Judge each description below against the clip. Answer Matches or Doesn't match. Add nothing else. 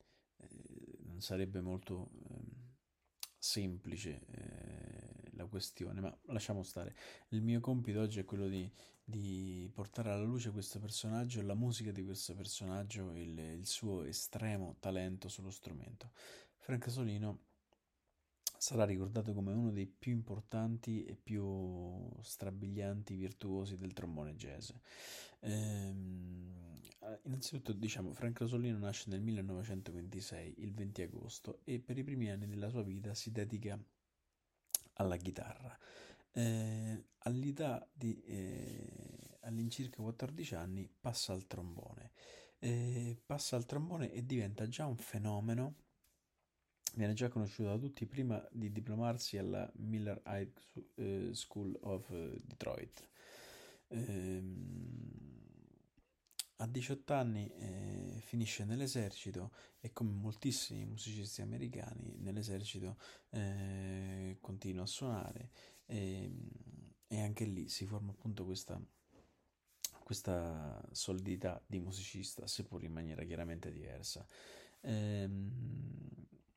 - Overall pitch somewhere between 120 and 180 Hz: Doesn't match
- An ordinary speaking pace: Doesn't match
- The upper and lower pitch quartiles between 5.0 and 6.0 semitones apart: Doesn't match